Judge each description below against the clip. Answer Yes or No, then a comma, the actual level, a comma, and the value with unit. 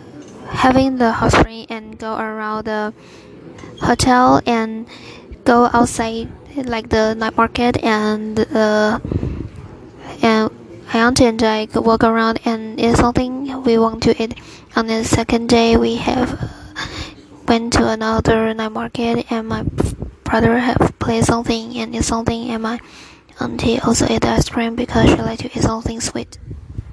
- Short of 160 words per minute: Yes, average, 150 wpm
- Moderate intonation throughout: No, narrow, 1.2 semitones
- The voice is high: Yes, high, 230 Hz